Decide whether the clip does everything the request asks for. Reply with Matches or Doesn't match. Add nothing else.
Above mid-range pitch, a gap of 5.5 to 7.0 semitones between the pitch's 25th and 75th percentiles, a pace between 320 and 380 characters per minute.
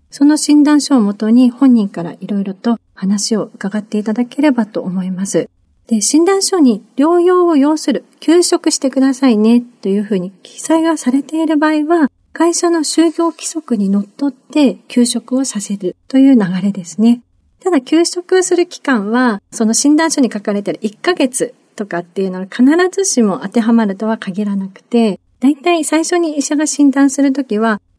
Matches